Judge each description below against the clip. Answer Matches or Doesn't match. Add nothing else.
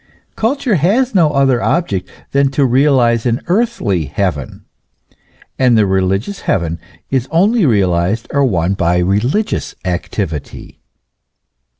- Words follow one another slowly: Matches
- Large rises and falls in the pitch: Matches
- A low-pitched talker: Matches